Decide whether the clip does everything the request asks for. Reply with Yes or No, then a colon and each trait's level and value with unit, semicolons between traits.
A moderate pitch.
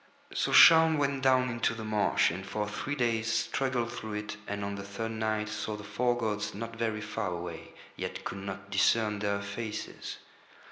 No: low, 110 Hz